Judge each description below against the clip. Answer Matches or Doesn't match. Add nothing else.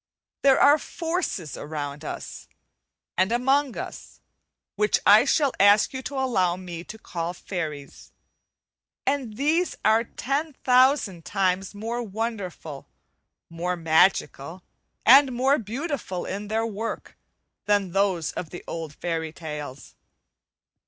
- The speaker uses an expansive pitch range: Matches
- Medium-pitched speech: Doesn't match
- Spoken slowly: Matches